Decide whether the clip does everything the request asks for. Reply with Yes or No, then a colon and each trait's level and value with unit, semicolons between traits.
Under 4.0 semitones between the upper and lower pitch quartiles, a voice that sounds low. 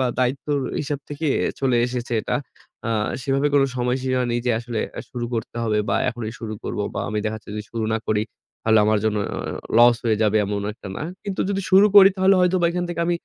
No: average, 5.1 semitones; low, 125 Hz